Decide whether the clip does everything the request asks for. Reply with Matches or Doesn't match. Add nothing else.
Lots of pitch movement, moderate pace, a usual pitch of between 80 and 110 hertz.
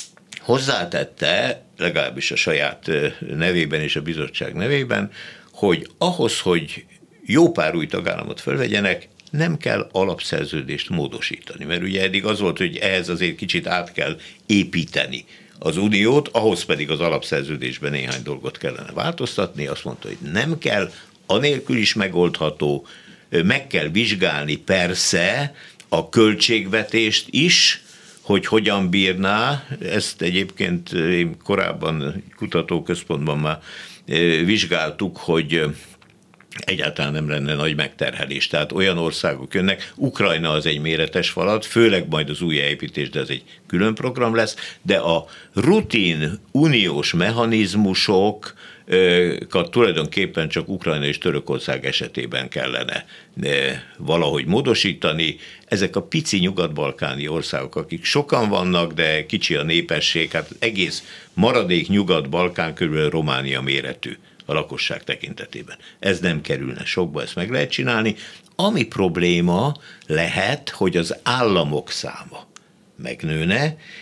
Matches